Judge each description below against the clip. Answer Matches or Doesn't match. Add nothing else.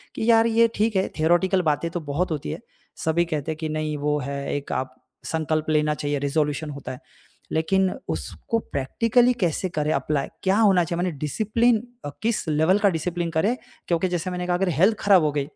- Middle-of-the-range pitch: Matches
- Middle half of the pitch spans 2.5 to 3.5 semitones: Doesn't match